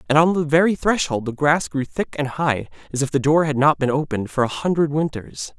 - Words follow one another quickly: Yes, fast, 245 wpm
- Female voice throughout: No, male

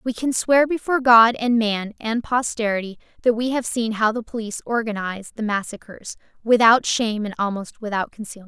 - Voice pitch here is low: No, high, 225 Hz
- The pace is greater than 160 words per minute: Yes, average, 175 wpm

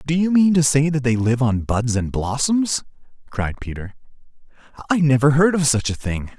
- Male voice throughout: Yes, male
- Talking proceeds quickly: No, average, 195 wpm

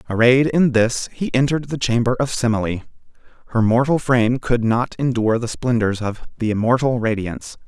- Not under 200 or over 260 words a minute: No, average, 165 wpm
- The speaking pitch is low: Yes, low, 120 Hz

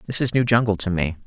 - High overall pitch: No, low, 105 Hz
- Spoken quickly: Yes, fast, 285 wpm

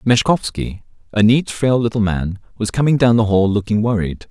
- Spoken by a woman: No, male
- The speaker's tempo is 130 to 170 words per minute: No, average, 180 wpm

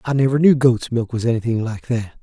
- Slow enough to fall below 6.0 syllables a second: Yes, 5.8 syllables/s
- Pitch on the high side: No, low, 120 Hz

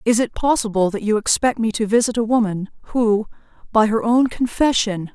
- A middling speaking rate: Yes, average, 185 wpm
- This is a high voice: Yes, high, 225 Hz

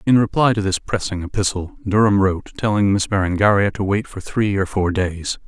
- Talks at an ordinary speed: Yes, average, 195 wpm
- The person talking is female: No, male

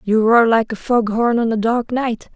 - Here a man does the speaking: No, female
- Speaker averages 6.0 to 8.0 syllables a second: No, 4.5 syllables/s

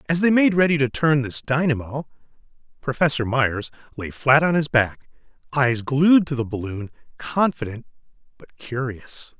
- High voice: No, low, 135 Hz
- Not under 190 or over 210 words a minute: No, average, 145 wpm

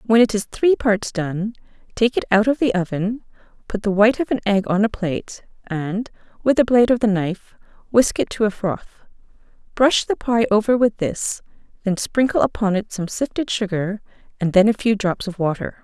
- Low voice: No, high, 210 Hz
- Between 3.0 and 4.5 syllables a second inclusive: No, 5.2 syllables/s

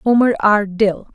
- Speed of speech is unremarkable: Yes, average, 155 wpm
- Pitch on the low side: No, high, 210 Hz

